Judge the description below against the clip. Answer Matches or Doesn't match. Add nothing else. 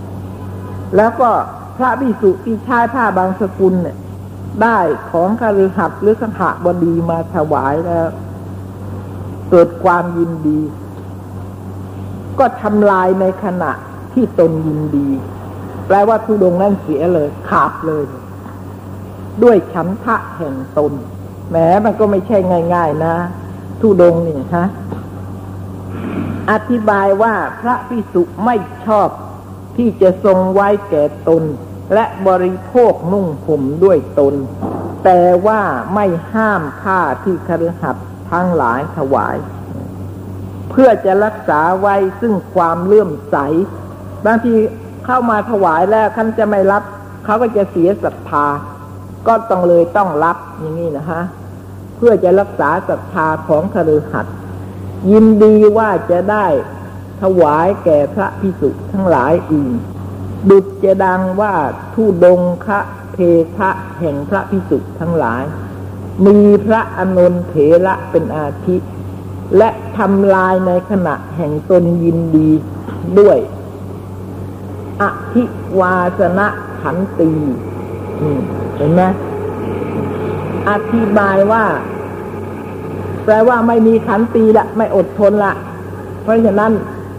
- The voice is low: Doesn't match